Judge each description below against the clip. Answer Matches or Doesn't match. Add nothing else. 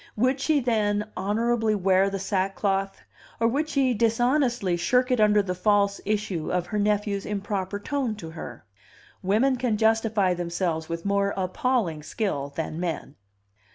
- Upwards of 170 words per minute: Doesn't match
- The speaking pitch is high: Matches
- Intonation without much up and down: Doesn't match